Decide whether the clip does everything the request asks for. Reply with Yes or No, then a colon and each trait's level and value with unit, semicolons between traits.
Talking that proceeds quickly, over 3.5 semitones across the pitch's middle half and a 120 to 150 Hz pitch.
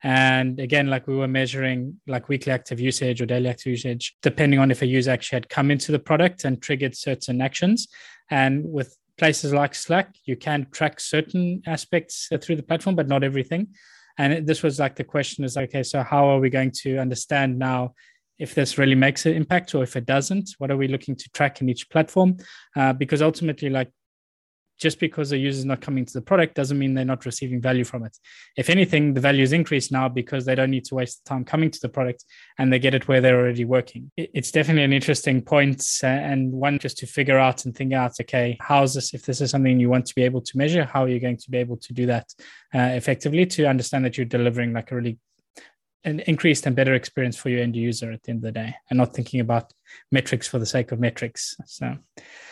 No: fast, 230 wpm; average, 2.7 semitones; low, 135 Hz